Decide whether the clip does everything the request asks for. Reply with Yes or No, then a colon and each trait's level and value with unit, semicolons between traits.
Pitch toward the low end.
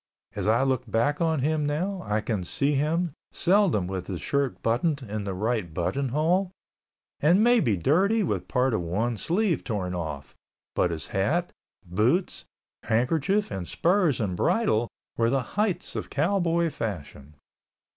Yes: low, 130 Hz